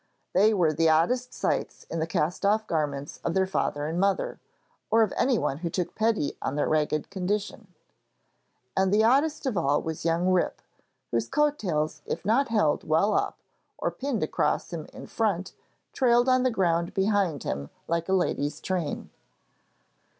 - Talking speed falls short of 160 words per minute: No, average, 170 wpm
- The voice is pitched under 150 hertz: No, medium, 185 Hz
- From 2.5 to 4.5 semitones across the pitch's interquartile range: No, wide, 5.6 semitones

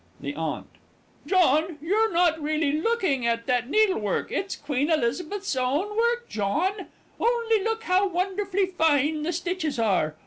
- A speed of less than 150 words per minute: Yes, average, 140 wpm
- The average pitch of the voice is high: Yes, very high, 335 Hz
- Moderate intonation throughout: No, wide, 6.3 semitones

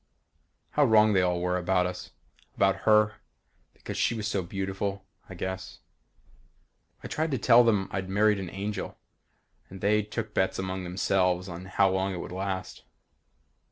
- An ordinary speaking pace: Yes, average, 160 wpm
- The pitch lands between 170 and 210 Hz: No, very low, 95 Hz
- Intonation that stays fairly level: Yes, narrow, 2.2 semitones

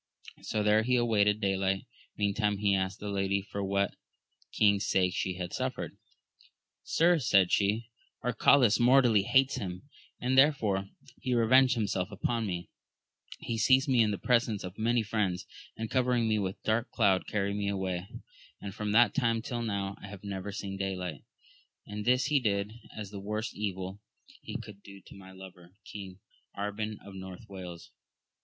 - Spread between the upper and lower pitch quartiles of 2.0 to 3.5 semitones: Yes, average, 2.9 semitones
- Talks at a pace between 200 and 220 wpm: No, average, 170 wpm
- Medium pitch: No, low, 105 Hz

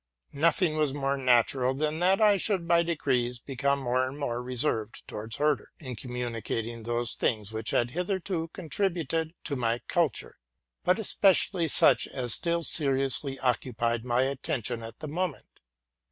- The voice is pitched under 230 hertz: Yes, low, 135 Hz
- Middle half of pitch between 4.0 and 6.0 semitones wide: Yes, wide, 5.4 semitones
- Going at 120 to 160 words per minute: Yes, average, 150 wpm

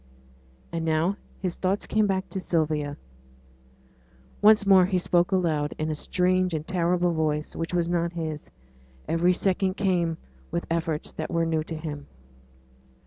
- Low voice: No, medium, 170 Hz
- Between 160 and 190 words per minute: No, average, 150 wpm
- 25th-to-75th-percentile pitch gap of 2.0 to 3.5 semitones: Yes, narrow, 2.6 semitones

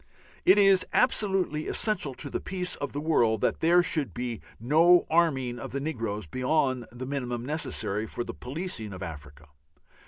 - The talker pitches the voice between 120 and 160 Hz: Yes, low, 135 Hz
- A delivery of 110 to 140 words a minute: No, average, 165 wpm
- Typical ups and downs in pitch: No, wide, 6.3 semitones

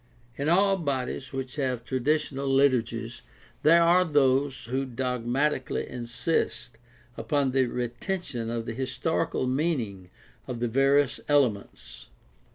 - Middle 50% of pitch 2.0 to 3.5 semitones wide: Yes, average, 3.2 semitones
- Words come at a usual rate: No, slow, 120 wpm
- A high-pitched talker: No, low, 130 Hz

